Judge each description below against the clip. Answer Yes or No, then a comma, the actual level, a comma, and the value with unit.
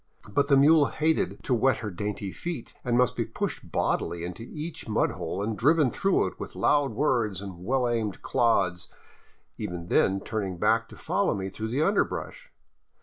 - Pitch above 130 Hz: No, low, 115 Hz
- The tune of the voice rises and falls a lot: Yes, wide, 6.2 semitones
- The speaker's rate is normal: Yes, average, 185 wpm